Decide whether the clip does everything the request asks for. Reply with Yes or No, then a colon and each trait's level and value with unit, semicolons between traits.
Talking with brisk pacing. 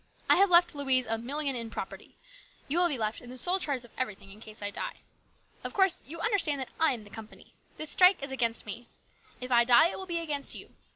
Yes: fast, 240 wpm